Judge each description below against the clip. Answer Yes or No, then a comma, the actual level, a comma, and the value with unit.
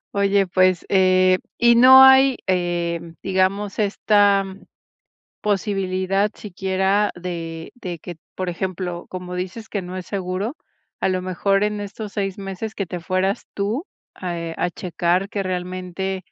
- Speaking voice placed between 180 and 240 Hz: Yes, high, 190 Hz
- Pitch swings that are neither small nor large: No, narrow, 1.9 semitones